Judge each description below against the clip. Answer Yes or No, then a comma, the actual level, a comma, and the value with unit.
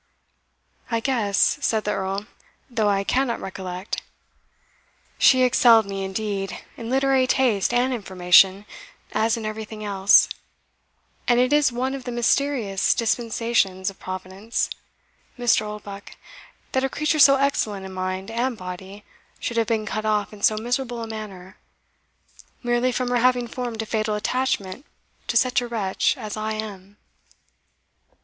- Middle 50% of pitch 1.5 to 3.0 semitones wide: No, average, 3.8 semitones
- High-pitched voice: Yes, high, 220 Hz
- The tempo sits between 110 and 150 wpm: Yes, average, 145 wpm